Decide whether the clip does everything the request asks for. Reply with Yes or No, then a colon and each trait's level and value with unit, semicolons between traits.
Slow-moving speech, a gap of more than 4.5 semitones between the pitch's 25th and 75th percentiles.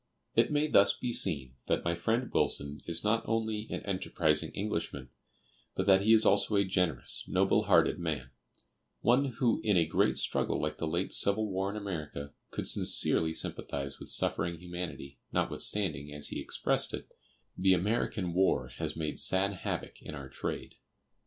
No: average, 165 wpm; average, 5.1 semitones